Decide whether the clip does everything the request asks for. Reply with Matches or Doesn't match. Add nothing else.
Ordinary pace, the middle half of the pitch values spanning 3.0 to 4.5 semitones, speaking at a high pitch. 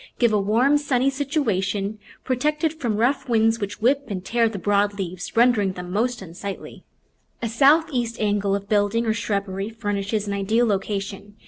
Matches